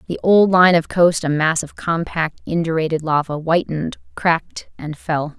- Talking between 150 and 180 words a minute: Yes, average, 165 wpm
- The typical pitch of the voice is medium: Yes, medium, 165 Hz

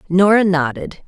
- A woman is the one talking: Yes, female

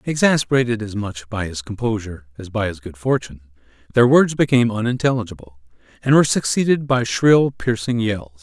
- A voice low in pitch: Yes, low, 110 Hz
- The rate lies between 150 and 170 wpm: Yes, average, 155 wpm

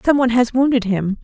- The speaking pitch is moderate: No, high, 240 Hz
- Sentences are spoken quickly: No, average, 195 wpm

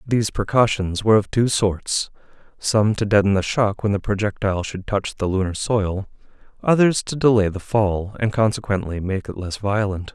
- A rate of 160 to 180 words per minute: Yes, average, 175 wpm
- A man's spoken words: Yes, male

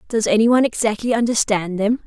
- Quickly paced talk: No, average, 175 wpm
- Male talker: No, female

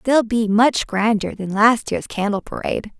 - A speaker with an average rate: Yes, average, 180 wpm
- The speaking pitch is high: Yes, high, 220 Hz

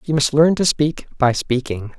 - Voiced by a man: Yes, male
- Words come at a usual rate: No, fast, 210 wpm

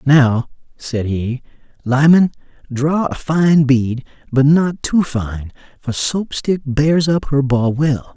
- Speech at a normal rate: Yes, average, 145 wpm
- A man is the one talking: Yes, male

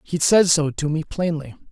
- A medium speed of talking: No, fast, 210 wpm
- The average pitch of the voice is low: No, medium, 160 Hz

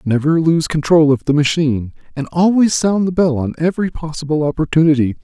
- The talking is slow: No, average, 170 wpm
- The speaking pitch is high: No, medium, 155 Hz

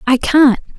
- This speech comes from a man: No, female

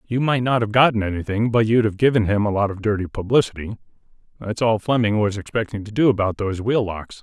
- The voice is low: Yes, low, 110 Hz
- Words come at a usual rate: No, fast, 225 wpm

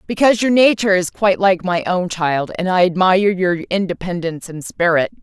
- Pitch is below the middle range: No, medium, 185 Hz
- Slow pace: No, average, 185 wpm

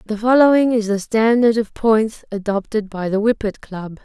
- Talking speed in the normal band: Yes, average, 180 wpm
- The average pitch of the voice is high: Yes, high, 220 Hz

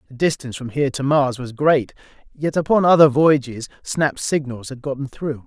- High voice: No, medium, 140 Hz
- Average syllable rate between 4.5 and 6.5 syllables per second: Yes, 5.2 syllables/s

